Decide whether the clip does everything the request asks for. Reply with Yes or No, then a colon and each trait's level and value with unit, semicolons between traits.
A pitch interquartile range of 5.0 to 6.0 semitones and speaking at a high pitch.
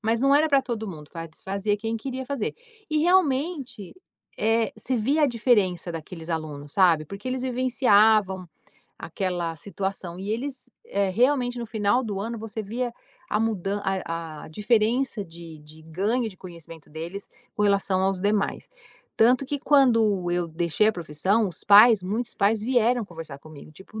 Yes: wide, 5.4 semitones; high, 210 Hz